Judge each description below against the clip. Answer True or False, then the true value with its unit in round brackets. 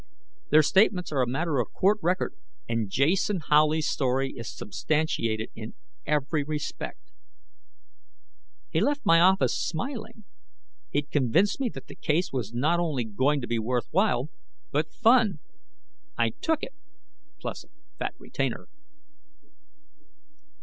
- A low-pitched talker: False (150 Hz)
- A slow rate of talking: True (130 wpm)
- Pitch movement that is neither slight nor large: False (6.7 semitones)